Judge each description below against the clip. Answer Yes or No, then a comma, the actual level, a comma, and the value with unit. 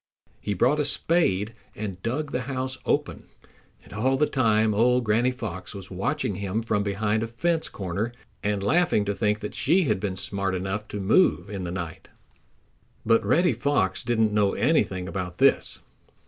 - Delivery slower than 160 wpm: No, average, 175 wpm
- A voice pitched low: Yes, low, 105 Hz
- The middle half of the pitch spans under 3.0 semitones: No, average, 4.5 semitones